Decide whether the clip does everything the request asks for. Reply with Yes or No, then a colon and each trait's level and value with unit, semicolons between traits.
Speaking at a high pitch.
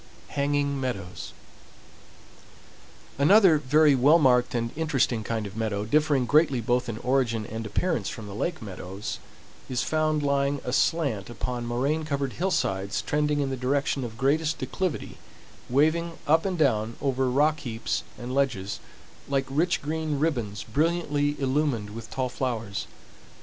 No: low, 135 Hz